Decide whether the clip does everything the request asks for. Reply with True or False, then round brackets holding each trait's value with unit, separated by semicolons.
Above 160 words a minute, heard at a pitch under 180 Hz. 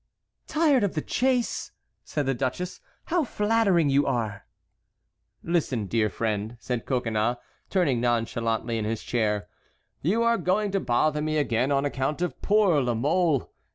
False (150 wpm; 140 Hz)